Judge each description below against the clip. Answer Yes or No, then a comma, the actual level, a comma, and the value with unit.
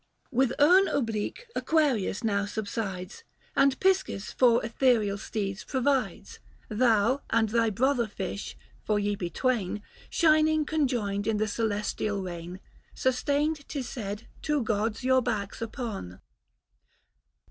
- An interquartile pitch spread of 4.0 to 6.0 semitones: Yes, average, 4.7 semitones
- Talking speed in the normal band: No, slow, 120 wpm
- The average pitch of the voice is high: Yes, high, 230 Hz